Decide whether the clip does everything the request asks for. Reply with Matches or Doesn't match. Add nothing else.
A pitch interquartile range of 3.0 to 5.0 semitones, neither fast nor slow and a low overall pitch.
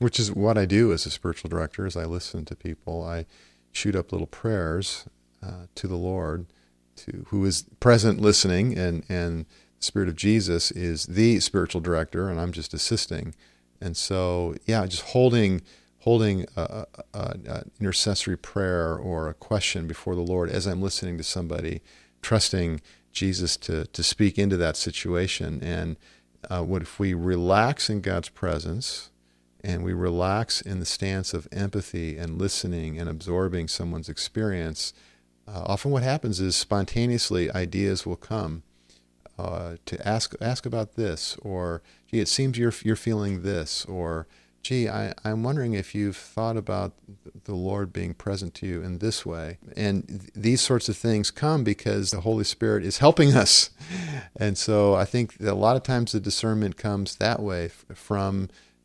Matches